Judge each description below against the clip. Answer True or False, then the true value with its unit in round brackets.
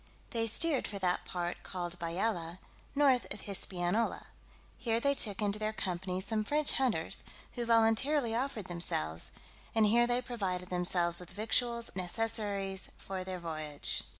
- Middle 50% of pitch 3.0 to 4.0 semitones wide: False (4.5 semitones)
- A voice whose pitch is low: False (205 Hz)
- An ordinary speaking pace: True (150 wpm)